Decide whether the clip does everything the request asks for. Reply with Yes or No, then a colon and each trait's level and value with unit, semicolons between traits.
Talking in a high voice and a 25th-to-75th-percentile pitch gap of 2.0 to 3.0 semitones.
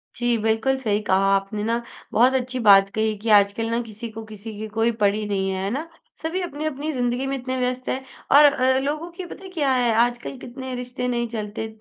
No: high, 240 Hz; average, 3.4 semitones